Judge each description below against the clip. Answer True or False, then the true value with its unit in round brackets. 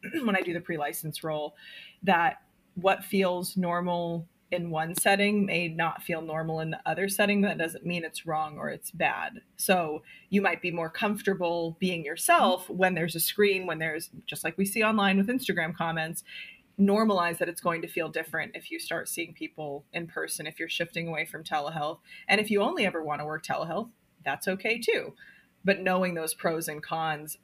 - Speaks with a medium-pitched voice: True (175 Hz)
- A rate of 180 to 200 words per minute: True (195 wpm)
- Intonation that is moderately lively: True (3.4 semitones)